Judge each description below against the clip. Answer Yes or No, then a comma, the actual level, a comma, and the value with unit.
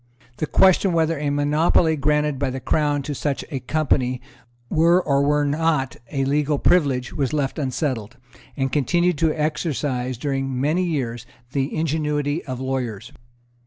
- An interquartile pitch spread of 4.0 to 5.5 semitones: No, narrow, 2.6 semitones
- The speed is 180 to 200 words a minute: No, average, 150 wpm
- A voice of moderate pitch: Yes, medium, 145 Hz